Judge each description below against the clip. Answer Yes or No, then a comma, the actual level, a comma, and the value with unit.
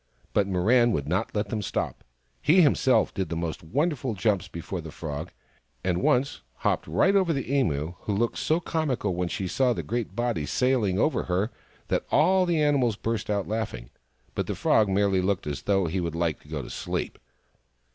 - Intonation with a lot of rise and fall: Yes, wide, 6.4 semitones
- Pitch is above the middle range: No, low, 105 Hz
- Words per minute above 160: Yes, average, 190 wpm